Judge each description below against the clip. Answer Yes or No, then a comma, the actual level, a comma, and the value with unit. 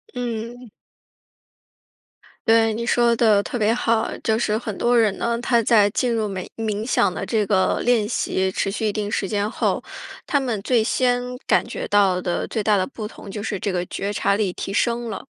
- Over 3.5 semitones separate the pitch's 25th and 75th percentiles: No, narrow, 2.5 semitones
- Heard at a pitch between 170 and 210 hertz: No, high, 220 Hz